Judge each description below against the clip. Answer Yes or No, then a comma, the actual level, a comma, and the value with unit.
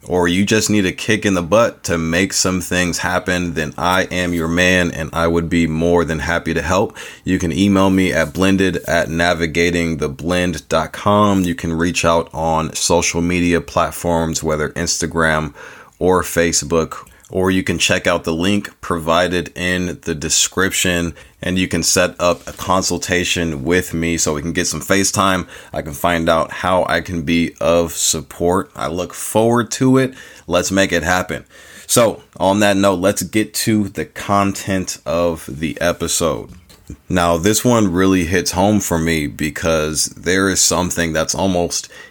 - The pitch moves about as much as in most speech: No, narrow, 2.1 semitones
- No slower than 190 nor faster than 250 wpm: No, average, 170 wpm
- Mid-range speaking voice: No, very low, 85 Hz